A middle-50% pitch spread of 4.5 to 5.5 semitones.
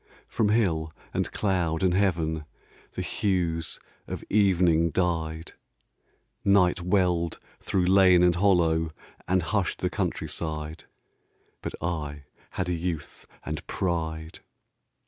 No: narrow, 2.5 semitones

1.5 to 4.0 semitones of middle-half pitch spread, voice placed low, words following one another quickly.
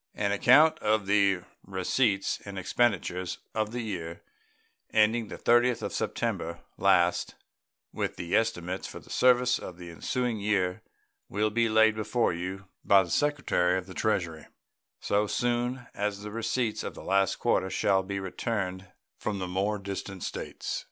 No: average, 3.3 semitones; low, 100 Hz; average, 155 wpm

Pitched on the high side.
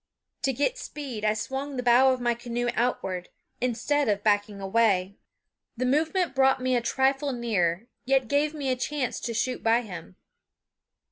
Yes: high, 245 Hz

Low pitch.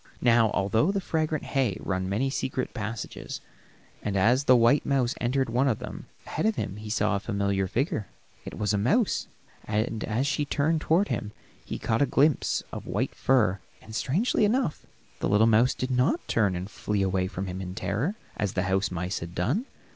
Yes: low, 115 Hz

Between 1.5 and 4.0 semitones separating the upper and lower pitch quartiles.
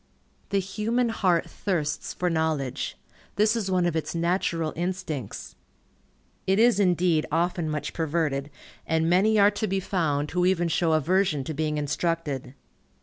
Yes: average, 3.5 semitones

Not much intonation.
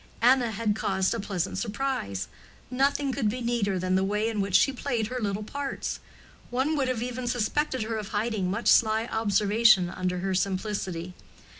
No: average, 4.0 semitones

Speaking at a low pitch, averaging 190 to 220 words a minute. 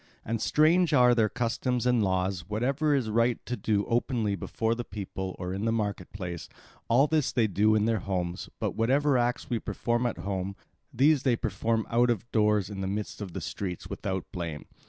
Yes: low, 110 Hz; average, 200 wpm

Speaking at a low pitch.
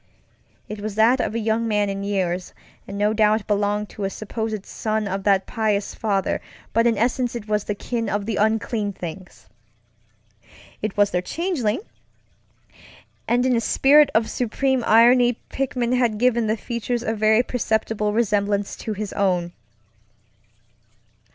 No: high, 215 Hz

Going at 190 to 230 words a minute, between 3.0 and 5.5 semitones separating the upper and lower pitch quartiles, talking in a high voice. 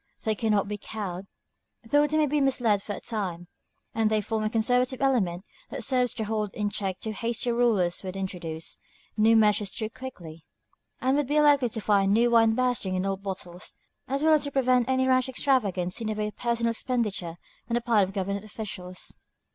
Yes: fast, 205 wpm; average, 4.2 semitones; high, 220 Hz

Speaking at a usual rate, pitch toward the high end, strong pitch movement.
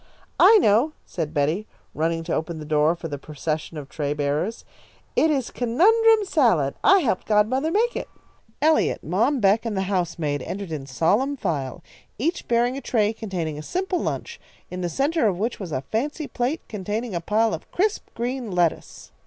Yes: average, 180 wpm; high, 210 Hz; wide, 8.5 semitones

